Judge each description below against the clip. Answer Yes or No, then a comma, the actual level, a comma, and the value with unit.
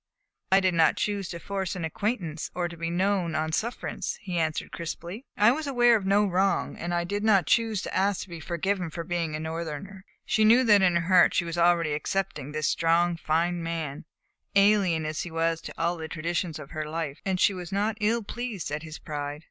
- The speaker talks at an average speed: No, fast, 220 wpm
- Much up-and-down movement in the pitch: No, average, 3.5 semitones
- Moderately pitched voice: Yes, medium, 175 Hz